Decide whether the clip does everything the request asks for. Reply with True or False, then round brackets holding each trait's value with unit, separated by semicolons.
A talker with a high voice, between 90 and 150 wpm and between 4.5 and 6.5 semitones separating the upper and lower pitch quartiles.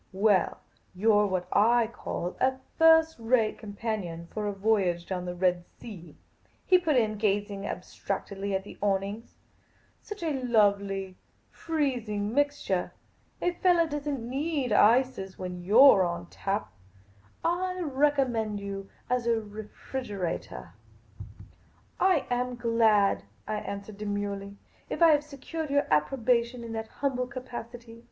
True (220 Hz; 145 wpm; 4.8 semitones)